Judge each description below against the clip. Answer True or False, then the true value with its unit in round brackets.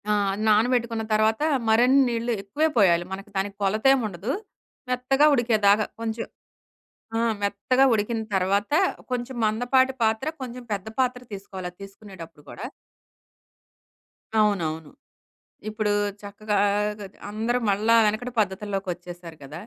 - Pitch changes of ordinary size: True (3.5 semitones)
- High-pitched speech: True (215 Hz)